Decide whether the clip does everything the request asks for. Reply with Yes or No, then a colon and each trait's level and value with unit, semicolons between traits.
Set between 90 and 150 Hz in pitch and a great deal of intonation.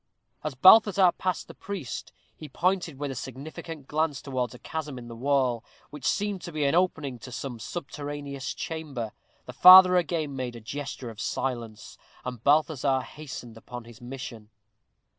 No: medium, 140 Hz; average, 4.5 semitones